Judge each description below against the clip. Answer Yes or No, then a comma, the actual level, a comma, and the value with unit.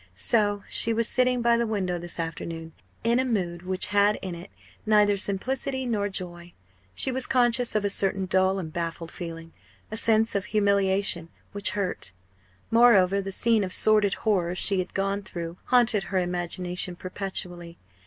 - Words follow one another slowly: No, average, 165 wpm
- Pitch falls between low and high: No, high, 195 Hz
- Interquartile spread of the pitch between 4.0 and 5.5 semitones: No, average, 3.6 semitones